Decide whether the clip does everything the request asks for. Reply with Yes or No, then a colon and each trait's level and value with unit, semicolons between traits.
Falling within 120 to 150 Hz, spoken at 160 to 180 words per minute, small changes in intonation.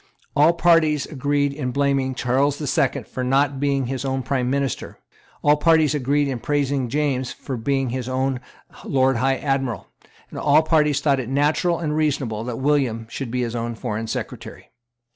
Yes: low, 135 Hz; average, 175 wpm; narrow, 2.3 semitones